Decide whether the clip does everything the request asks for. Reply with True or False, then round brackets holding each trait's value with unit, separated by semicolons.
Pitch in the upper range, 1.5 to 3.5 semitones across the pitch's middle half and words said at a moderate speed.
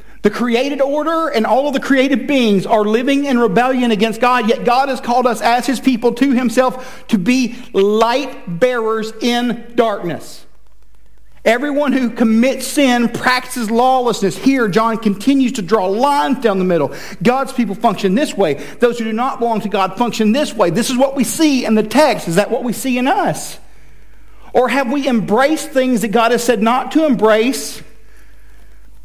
True (240 Hz; 2.9 semitones; 180 wpm)